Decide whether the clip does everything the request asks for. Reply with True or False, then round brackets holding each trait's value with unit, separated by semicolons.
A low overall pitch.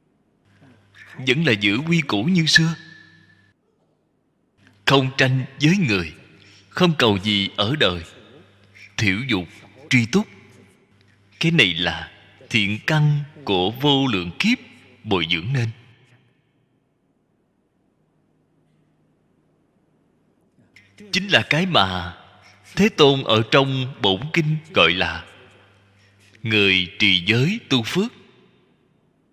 True (120 Hz)